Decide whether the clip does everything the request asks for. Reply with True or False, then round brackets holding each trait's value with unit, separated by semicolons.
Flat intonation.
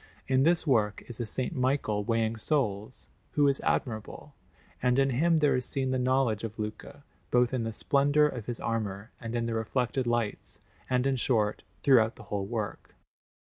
False (3.3 semitones)